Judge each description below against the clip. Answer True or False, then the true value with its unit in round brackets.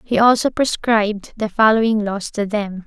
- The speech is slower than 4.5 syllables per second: False (4.7 syllables/s)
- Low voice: False (215 Hz)